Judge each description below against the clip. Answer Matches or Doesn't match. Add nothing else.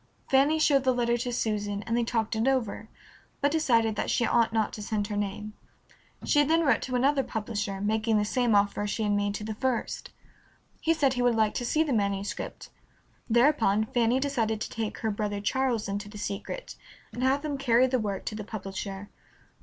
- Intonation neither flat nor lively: Matches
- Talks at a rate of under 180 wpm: Doesn't match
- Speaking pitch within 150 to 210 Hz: Doesn't match